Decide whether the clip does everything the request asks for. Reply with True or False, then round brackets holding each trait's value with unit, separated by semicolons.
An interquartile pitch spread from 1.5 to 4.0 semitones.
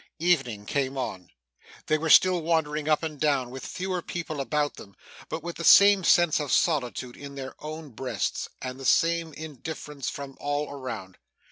True (3.5 semitones)